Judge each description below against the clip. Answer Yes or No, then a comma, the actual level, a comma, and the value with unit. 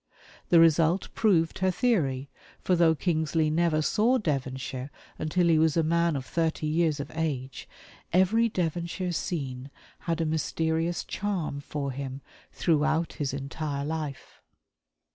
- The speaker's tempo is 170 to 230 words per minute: No, slow, 135 wpm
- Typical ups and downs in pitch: Yes, average, 3.1 semitones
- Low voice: No, medium, 160 Hz